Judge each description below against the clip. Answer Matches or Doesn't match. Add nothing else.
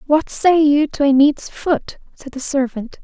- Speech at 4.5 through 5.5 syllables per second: Doesn't match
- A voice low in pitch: Doesn't match